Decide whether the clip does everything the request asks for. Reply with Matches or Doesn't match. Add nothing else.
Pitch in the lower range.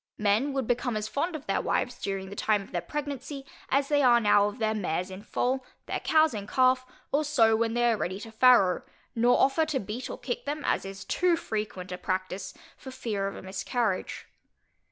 Doesn't match